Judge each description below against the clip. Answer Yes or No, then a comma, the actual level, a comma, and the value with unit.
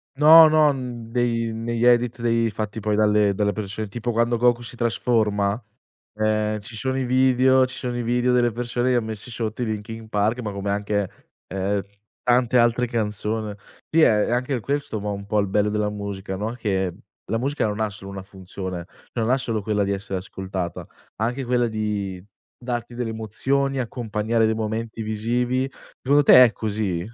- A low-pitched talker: Yes, low, 110 Hz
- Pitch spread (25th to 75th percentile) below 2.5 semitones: No, average, 2.8 semitones